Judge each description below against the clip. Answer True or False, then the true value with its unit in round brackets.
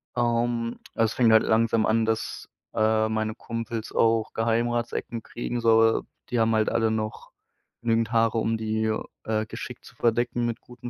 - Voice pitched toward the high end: False (115 Hz)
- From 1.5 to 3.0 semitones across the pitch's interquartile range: False (1.0 semitones)